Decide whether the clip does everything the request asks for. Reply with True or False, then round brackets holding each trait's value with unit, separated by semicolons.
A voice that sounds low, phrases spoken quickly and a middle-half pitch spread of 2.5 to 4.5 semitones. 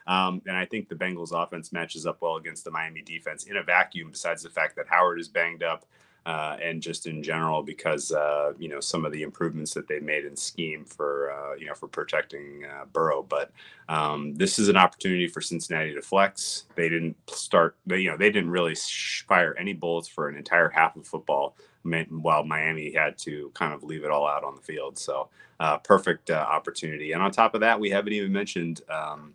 True (80 Hz; 215 wpm; 2.9 semitones)